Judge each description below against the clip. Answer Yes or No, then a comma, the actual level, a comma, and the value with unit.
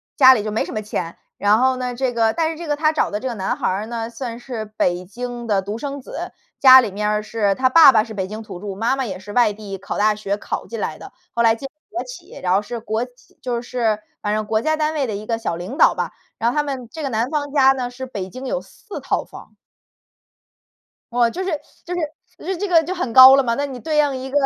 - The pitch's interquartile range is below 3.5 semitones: No, average, 4.3 semitones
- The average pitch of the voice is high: Yes, high, 240 Hz